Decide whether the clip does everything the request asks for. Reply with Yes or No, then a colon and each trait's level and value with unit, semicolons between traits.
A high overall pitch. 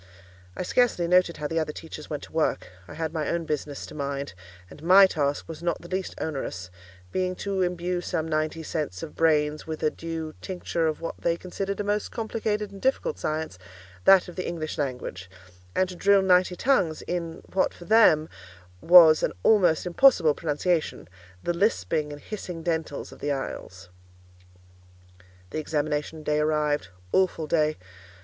No: medium, 165 Hz